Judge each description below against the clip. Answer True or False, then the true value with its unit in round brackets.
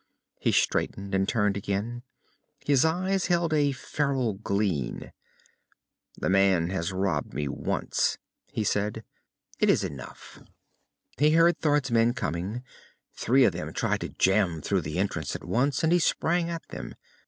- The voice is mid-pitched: False (110 Hz)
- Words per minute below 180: True (150 wpm)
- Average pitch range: False (7.4 semitones)